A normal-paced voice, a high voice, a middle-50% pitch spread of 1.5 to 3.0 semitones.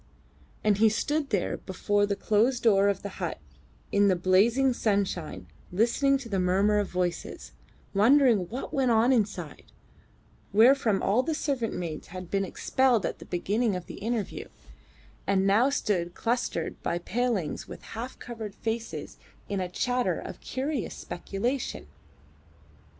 No: average, 150 wpm; high, 210 Hz; average, 4.2 semitones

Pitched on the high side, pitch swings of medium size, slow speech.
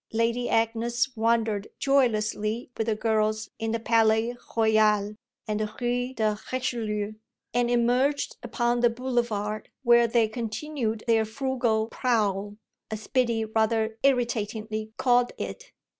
No: high, 225 Hz; narrow, 2.0 semitones; slow, 125 wpm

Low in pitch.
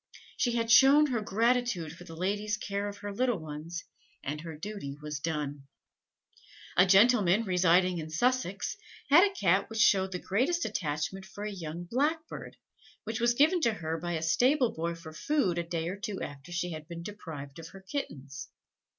No: high, 190 Hz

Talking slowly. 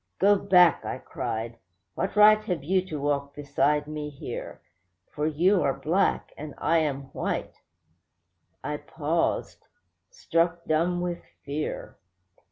Yes: slow, 130 wpm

